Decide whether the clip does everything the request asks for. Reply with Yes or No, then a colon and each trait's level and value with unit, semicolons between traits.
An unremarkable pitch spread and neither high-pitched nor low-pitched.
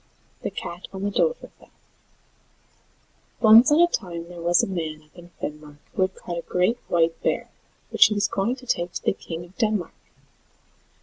Yes: average, 4.1 semitones; medium, 180 Hz